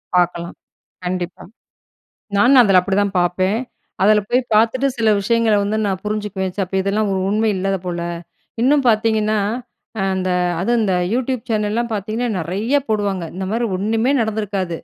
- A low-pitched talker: No, high, 210 Hz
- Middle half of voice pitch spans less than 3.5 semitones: Yes, average, 3.1 semitones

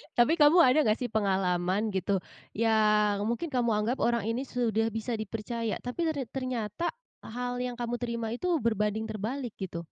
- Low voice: No, high, 230 Hz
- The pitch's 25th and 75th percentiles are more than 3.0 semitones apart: No, average, 2.7 semitones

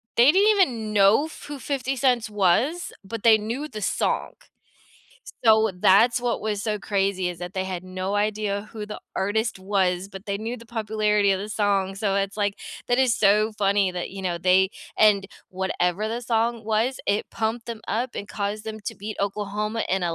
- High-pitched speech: Yes, high, 210 Hz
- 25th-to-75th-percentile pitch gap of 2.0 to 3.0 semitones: Yes, narrow, 2.6 semitones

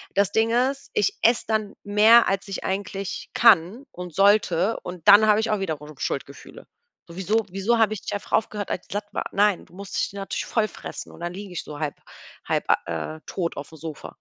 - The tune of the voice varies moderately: Yes, average, 3.6 semitones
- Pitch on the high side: Yes, high, 200 Hz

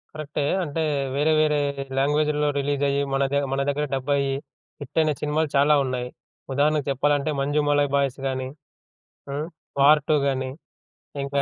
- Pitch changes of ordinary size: No, narrow, 1.4 semitones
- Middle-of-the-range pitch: Yes, medium, 145 Hz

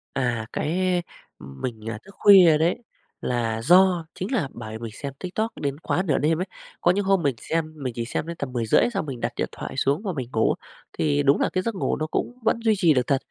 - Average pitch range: No, wide, 6.6 semitones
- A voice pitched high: No, medium, 150 Hz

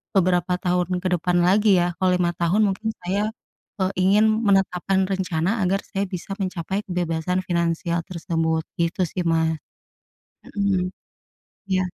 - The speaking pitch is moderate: Yes, medium, 180 Hz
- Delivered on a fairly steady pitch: Yes, narrow, 2.0 semitones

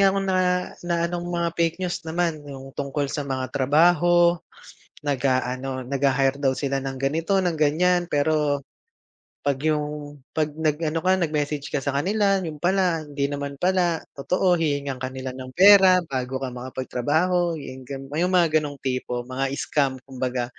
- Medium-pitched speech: Yes, medium, 145 Hz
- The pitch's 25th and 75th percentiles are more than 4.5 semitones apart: No, average, 4.2 semitones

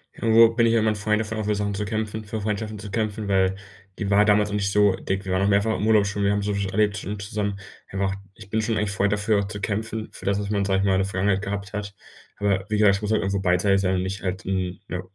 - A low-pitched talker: Yes, low, 100 Hz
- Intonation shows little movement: Yes, narrow, 1.4 semitones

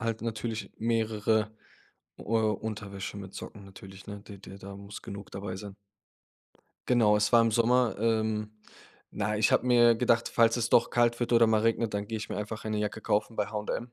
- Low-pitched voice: Yes, low, 110 Hz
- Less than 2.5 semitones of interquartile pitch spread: Yes, narrow, 1.9 semitones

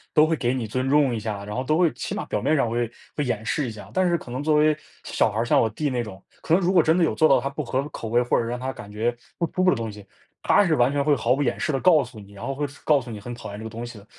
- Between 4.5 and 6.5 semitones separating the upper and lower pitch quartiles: Yes, average, 4.8 semitones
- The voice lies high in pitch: No, low, 125 Hz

